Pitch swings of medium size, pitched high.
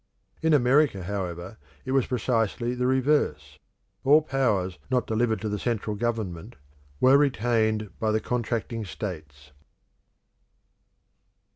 No: average, 4.2 semitones; low, 115 Hz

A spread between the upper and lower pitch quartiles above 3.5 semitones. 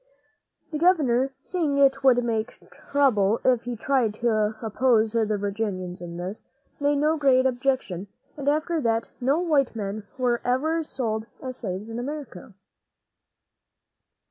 Yes: average, 4.5 semitones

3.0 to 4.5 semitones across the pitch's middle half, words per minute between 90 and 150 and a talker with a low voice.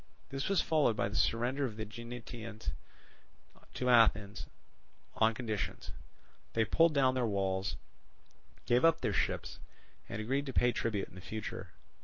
Yes: average, 3.3 semitones; average, 145 wpm; low, 115 Hz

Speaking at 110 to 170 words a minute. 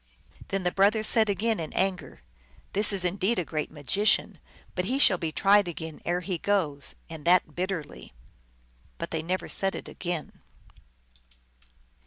Yes: average, 165 wpm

